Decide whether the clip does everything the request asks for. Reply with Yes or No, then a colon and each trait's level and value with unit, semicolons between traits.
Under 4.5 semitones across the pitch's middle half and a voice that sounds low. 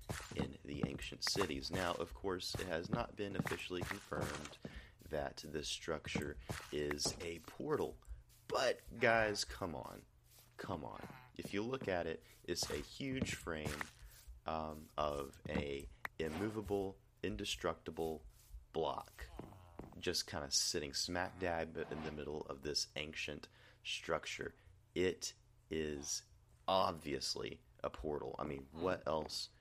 No: wide, 5.4 semitones; very low, 80 Hz